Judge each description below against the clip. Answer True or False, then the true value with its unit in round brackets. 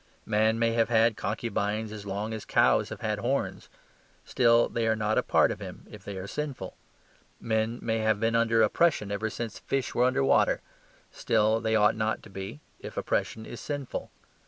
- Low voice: True (110 Hz)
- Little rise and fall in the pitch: True (1.6 semitones)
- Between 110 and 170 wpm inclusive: False (190 wpm)